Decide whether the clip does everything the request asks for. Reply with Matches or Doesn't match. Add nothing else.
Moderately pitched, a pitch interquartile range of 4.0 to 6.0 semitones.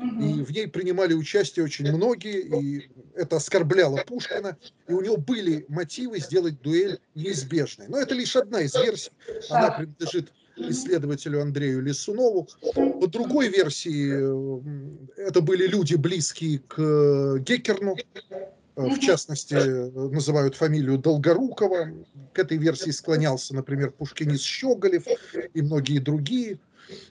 Matches